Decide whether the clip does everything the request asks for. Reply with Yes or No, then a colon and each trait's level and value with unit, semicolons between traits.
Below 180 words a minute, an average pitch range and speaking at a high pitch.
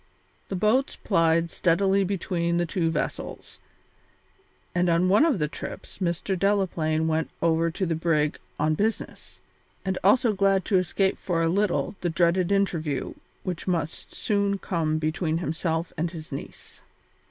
No: average, 150 wpm; average, 3.2 semitones; medium, 175 Hz